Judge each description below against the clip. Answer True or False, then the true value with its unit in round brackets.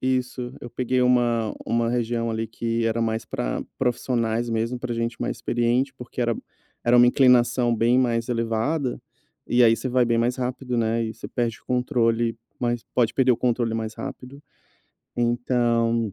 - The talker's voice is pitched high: False (120 Hz)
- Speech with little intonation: True (1.4 semitones)